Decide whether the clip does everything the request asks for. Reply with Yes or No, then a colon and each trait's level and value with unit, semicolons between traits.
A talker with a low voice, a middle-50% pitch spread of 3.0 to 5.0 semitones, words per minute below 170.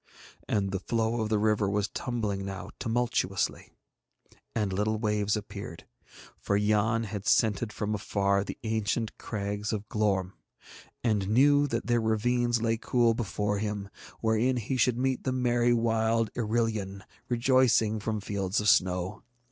No: low, 110 Hz; narrow, 2.4 semitones; average, 145 wpm